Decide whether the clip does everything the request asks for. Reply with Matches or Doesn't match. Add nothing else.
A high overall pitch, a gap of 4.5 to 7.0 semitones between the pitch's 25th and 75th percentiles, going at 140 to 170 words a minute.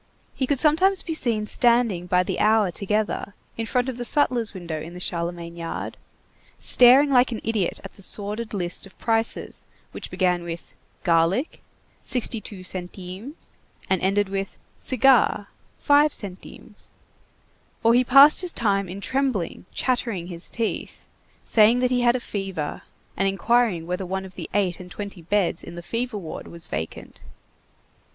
Matches